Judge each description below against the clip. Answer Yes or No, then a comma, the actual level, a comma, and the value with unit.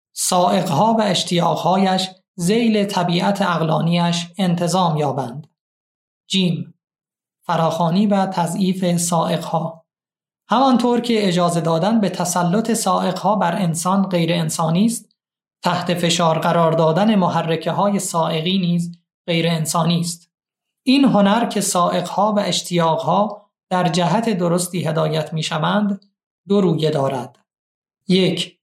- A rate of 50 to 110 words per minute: Yes, slow, 105 wpm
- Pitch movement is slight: No, average, 3.1 semitones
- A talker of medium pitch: Yes, medium, 175 Hz